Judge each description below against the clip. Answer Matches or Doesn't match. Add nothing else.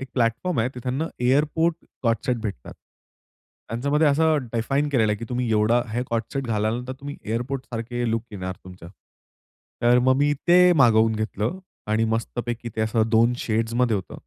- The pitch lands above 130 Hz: Doesn't match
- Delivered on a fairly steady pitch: Doesn't match